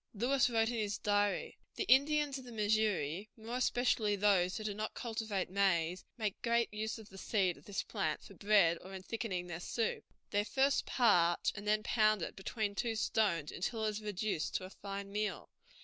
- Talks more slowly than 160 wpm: No, average, 195 wpm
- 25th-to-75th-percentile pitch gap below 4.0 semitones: Yes, average, 2.7 semitones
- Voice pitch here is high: Yes, high, 210 Hz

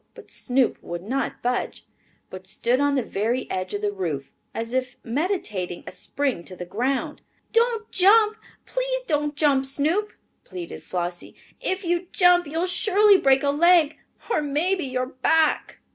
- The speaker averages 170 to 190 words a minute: No, average, 160 wpm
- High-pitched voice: Yes, very high, 275 Hz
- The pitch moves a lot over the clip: Yes, wide, 8.2 semitones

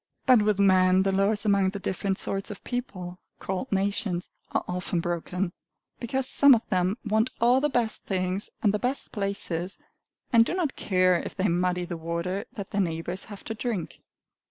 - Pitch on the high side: Yes, high, 195 Hz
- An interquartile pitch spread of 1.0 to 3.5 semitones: Yes, average, 3.2 semitones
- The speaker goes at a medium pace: Yes, average, 180 wpm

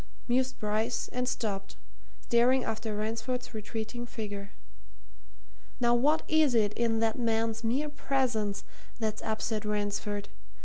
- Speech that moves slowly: Yes, slow, 120 wpm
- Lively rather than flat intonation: No, narrow, 2.5 semitones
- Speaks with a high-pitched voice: Yes, high, 225 Hz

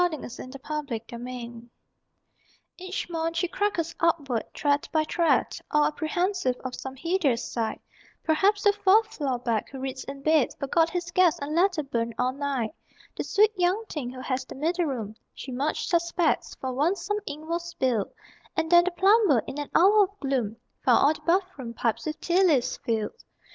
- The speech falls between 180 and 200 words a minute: Yes, average, 190 wpm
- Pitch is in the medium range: No, very high, 305 Hz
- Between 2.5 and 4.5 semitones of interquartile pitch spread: No, wide, 5.5 semitones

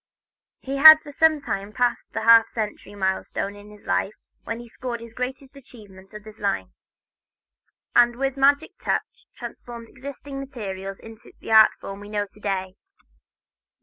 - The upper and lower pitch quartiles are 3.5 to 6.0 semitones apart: Yes, average, 4.4 semitones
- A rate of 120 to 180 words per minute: Yes, average, 160 wpm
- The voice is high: Yes, high, 225 Hz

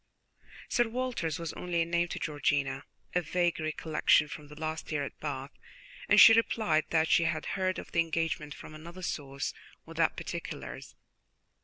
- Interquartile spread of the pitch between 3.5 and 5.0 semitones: No, narrow, 2.5 semitones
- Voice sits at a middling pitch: Yes, medium, 160 Hz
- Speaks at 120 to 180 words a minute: Yes, average, 165 wpm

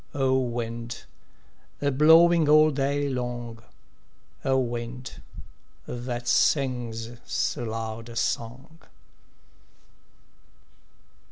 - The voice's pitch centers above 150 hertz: No, low, 125 Hz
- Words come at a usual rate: No, slow, 80 wpm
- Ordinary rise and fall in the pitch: Yes, average, 3.1 semitones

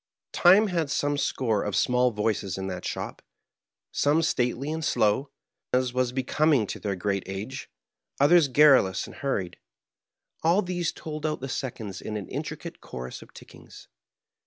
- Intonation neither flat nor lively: No, wide, 6.6 semitones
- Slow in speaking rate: No, average, 155 wpm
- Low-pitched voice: Yes, low, 130 Hz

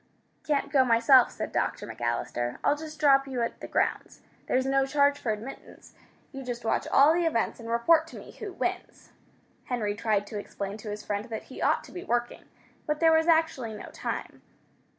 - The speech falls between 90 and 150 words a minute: No, average, 195 wpm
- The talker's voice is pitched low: No, very high, 260 Hz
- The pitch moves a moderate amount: Yes, average, 4.9 semitones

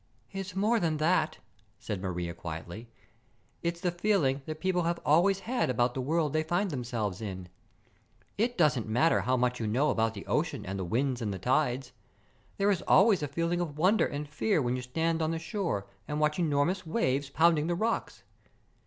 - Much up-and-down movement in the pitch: Yes, wide, 6.0 semitones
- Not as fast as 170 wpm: No, average, 190 wpm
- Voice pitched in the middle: Yes, medium, 150 Hz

